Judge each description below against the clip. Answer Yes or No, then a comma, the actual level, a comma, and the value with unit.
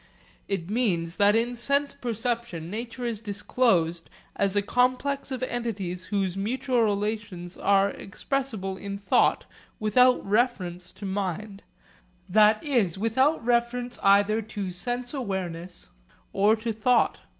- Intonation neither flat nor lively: Yes, average, 3.9 semitones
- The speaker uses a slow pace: Yes, slow, 125 wpm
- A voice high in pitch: Yes, high, 215 Hz